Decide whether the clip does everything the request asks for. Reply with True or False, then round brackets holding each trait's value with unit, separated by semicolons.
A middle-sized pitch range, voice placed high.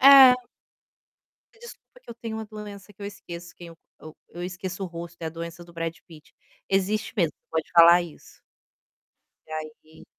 False (3.8 semitones; 175 Hz)